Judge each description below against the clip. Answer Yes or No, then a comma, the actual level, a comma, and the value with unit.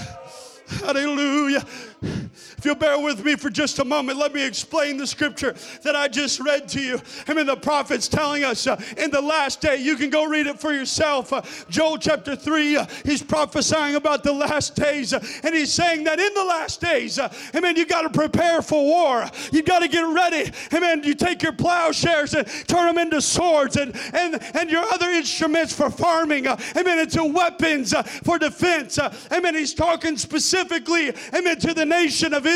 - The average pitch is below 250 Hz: No, very high, 305 Hz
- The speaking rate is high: Yes, fast, 210 wpm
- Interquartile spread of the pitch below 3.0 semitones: Yes, narrow, 2.5 semitones